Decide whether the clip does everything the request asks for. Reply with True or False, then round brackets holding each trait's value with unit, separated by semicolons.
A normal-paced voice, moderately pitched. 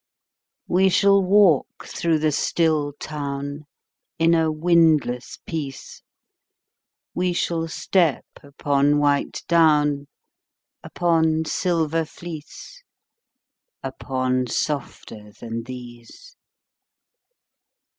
False (80 wpm; 155 Hz)